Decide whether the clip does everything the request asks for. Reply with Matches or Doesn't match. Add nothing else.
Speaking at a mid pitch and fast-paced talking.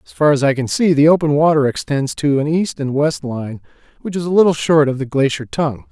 Matches